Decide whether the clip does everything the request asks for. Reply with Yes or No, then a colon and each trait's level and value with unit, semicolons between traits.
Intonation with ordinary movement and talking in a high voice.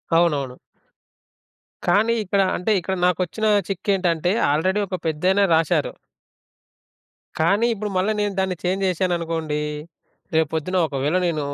No: average, 3.1 semitones; medium, 180 Hz